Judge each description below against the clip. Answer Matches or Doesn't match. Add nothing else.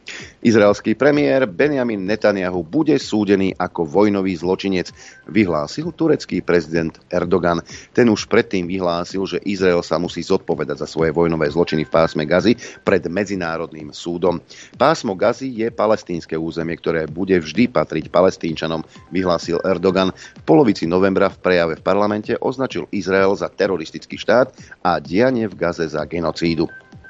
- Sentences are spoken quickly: Doesn't match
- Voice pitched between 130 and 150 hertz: Doesn't match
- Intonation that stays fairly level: Doesn't match